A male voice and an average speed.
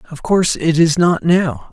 No: male; fast, 210 wpm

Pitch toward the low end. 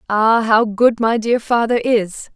No: high, 225 Hz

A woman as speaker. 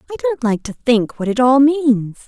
Yes: female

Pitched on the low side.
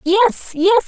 No: very high, 385 Hz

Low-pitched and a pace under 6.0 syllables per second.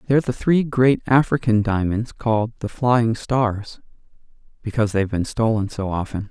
Yes: low, 115 Hz; 5.0 syllables/s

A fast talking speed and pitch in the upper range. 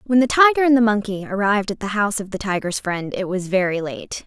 Yes: fast, 255 wpm; high, 210 Hz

